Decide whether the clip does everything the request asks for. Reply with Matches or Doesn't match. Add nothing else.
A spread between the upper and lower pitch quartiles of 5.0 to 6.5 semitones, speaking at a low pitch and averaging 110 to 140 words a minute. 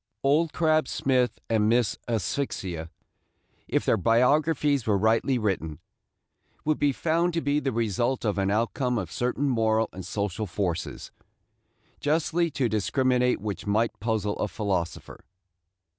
Matches